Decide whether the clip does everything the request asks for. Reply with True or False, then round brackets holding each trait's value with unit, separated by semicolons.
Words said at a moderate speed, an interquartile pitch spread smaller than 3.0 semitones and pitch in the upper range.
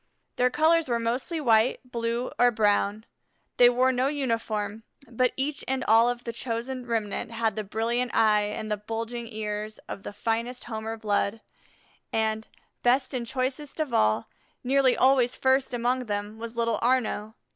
True (160 wpm; 2.5 semitones; 235 Hz)